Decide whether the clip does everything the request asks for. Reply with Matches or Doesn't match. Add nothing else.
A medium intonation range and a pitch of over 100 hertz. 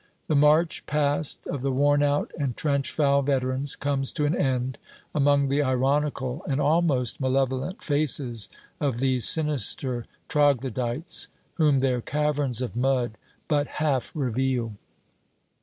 Doesn't match